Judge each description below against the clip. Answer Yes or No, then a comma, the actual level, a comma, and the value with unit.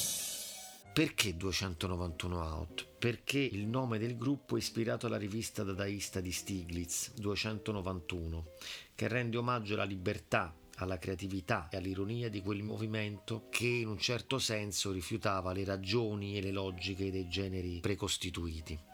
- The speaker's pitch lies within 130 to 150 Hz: No, low, 100 Hz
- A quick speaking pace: No, average, 135 wpm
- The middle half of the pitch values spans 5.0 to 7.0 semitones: No, average, 3.2 semitones